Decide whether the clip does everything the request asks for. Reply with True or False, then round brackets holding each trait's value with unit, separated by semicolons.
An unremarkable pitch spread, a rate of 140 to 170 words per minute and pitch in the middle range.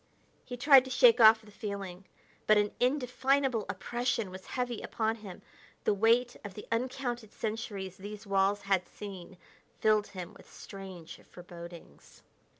False (3.9 semitones; 145 wpm; 210 Hz)